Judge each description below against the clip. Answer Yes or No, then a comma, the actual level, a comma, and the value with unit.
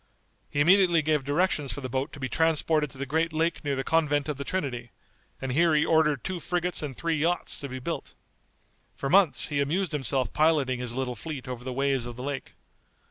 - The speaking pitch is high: No, medium, 145 Hz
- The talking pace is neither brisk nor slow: No, fast, 215 wpm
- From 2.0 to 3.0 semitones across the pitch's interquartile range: No, average, 3.6 semitones